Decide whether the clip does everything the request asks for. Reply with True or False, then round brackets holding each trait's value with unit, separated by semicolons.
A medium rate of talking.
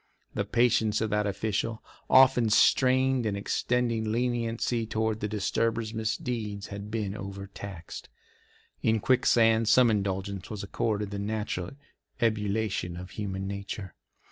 False (120 wpm)